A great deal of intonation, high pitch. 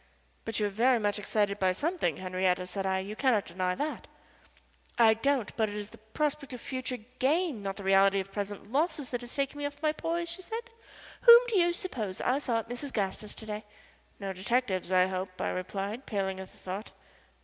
Yes: wide, 6.2 semitones; high, 215 Hz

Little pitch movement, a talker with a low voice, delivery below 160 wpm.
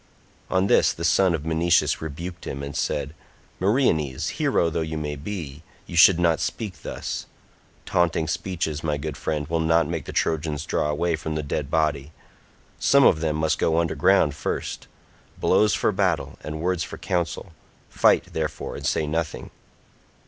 No: narrow, 2.2 semitones; very low, 80 Hz; average, 165 wpm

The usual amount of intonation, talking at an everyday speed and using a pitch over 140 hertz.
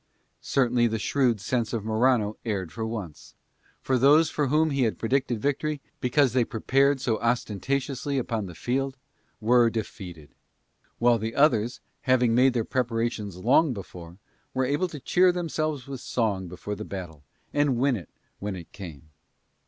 No: average, 4.4 semitones; average, 160 wpm; low, 120 Hz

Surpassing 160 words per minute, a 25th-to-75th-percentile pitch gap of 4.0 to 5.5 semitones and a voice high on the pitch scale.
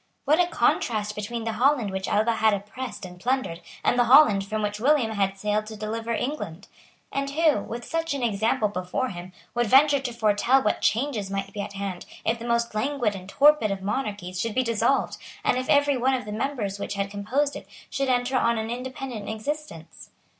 Yes: fast, 205 wpm; average, 4.3 semitones; high, 225 Hz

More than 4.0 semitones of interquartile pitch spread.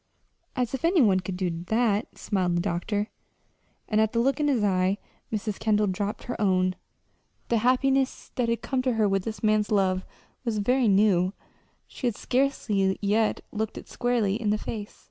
No: average, 3.7 semitones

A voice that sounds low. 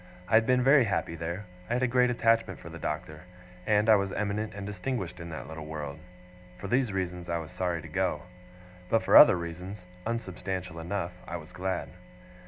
Yes: very low, 95 Hz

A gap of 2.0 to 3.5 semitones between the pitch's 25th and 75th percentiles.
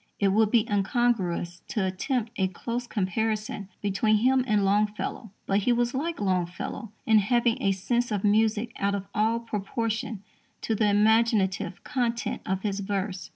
Yes: average, 2.9 semitones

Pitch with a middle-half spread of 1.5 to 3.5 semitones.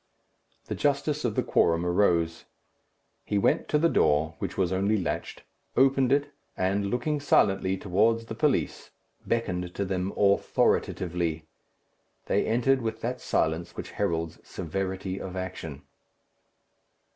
No: average, 5.0 semitones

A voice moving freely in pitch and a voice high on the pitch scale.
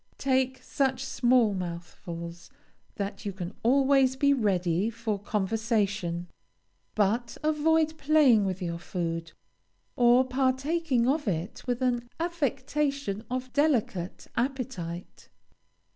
Yes: wide, 5.8 semitones; high, 240 Hz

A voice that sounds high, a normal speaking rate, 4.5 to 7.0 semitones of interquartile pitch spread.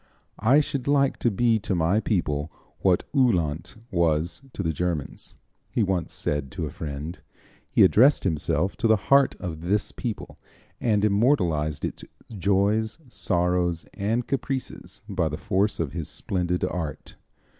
No: very low, 95 Hz; average, 145 wpm; average, 5.1 semitones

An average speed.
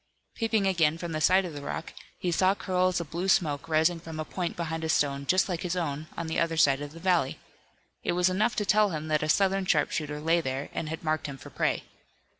No: fast, 240 wpm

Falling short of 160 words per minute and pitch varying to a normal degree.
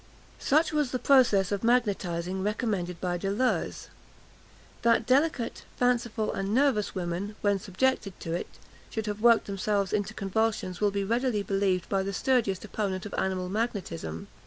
Yes: average, 150 wpm; average, 3.6 semitones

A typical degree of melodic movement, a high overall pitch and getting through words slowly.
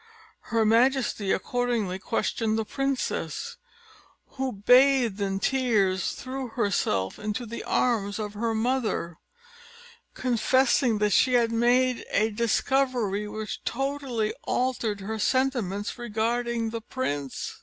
Yes: average, 3.4 semitones; high, 230 Hz; slow, 110 wpm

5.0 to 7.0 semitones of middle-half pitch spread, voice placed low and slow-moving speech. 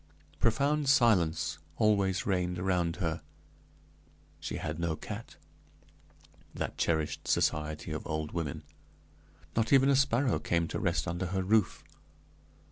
Yes: wide, 5.6 semitones; very low, 90 Hz; slow, 125 wpm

